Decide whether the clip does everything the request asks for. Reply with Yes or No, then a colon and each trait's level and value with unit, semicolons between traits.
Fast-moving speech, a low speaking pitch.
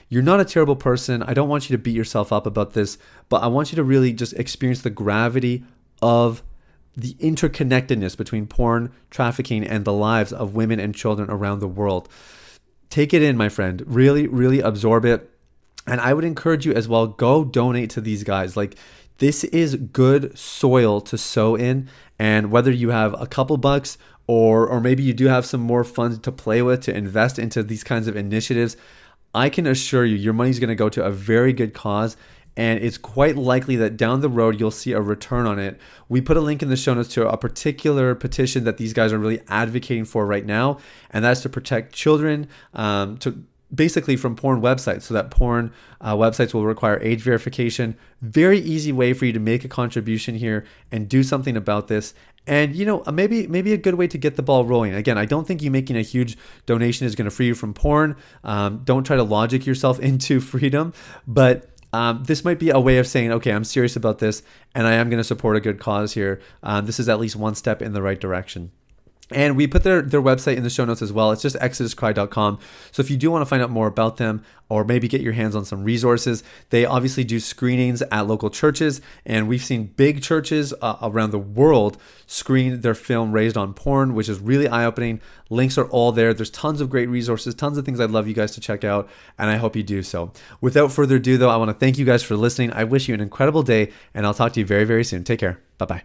Yes: fast, 230 wpm; low, 120 Hz